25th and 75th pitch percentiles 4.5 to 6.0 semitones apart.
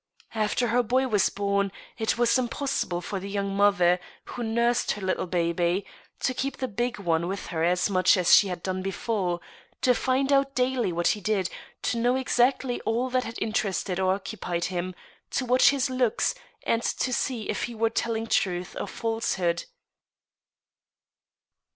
Yes: average, 4.8 semitones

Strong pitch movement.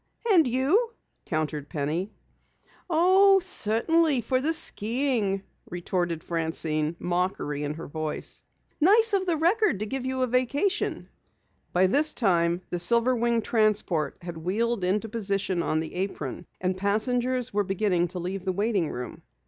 Yes: wide, 6.9 semitones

